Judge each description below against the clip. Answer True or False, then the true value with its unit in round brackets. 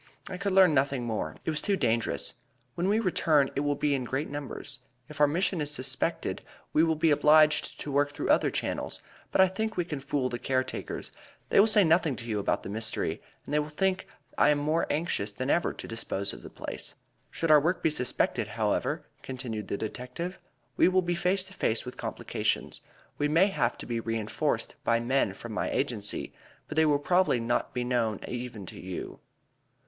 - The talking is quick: True (210 wpm)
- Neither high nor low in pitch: True (145 Hz)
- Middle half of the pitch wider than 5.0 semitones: True (5.6 semitones)